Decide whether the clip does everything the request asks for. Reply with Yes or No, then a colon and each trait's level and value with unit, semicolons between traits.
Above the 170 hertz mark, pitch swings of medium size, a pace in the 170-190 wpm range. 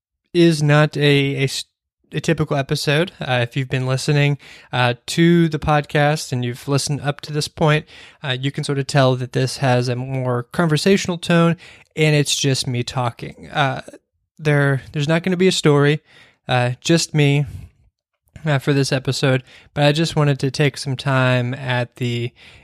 No: medium, 140 Hz; average, 3.2 semitones; average, 180 wpm